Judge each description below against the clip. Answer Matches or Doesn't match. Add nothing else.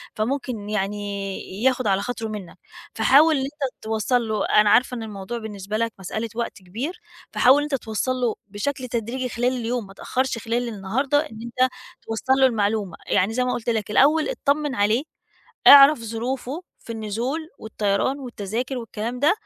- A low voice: Doesn't match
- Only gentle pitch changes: Doesn't match